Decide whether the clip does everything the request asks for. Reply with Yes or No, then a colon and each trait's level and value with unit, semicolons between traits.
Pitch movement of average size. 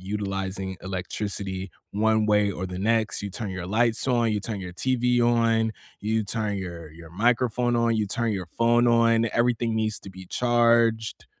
Yes: average, 3.4 semitones